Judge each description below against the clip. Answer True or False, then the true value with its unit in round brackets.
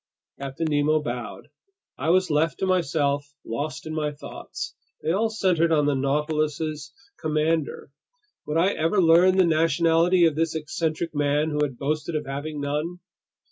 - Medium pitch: True (155 Hz)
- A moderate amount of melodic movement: False (2.2 semitones)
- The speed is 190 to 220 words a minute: False (155 wpm)